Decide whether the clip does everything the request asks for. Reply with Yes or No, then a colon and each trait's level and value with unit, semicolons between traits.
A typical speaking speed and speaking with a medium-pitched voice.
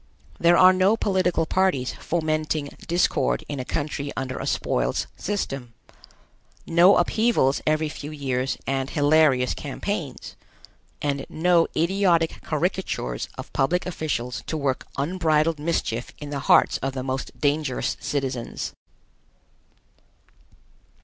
No: slow, 115 wpm; medium, 150 Hz